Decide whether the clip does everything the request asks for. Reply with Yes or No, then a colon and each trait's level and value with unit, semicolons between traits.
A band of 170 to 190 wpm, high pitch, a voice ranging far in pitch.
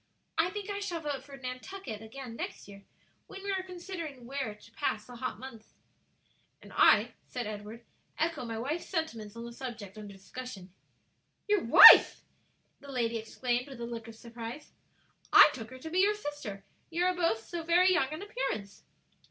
Yes: average, 180 wpm; very high, 255 Hz; wide, 6.9 semitones